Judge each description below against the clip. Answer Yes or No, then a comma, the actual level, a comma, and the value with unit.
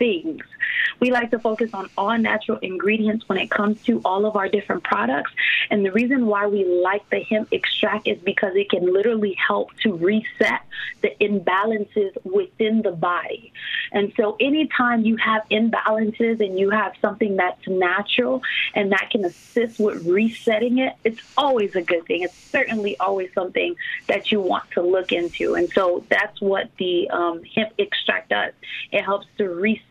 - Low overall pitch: No, high, 215 Hz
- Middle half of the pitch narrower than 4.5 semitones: Yes, average, 3.2 semitones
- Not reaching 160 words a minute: No, average, 175 wpm